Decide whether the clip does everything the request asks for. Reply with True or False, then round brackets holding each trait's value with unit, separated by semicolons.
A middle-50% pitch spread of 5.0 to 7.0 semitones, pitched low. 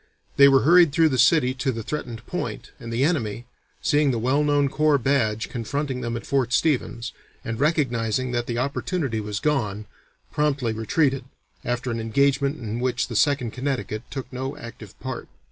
False (3.5 semitones; 130 Hz)